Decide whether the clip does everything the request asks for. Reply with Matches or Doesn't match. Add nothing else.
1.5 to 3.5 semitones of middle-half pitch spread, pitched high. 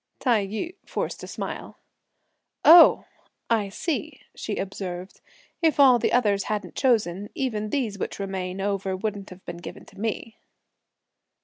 Doesn't match